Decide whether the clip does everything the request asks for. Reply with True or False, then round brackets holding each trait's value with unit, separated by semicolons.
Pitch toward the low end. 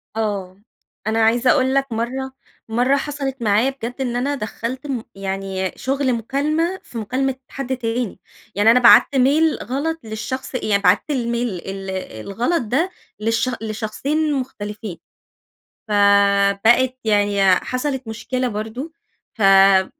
False (235 Hz)